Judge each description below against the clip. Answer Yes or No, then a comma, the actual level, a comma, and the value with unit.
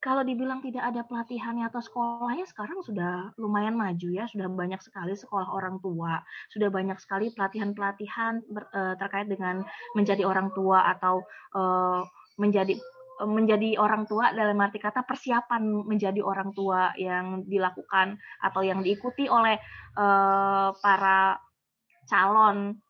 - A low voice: No, high, 200 Hz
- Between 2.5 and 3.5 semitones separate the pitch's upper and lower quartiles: Yes, average, 2.9 semitones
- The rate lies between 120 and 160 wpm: Yes, average, 135 wpm